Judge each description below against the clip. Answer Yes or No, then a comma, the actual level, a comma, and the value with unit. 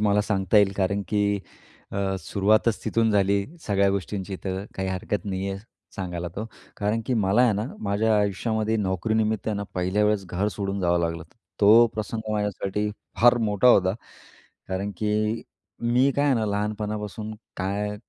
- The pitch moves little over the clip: Yes, narrow, 1.9 semitones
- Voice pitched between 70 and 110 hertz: Yes, low, 105 Hz